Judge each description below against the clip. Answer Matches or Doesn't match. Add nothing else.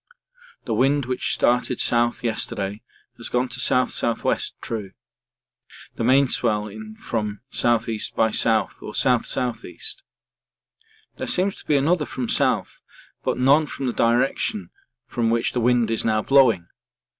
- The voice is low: Matches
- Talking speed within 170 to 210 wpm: Doesn't match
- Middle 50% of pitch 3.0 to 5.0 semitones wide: Doesn't match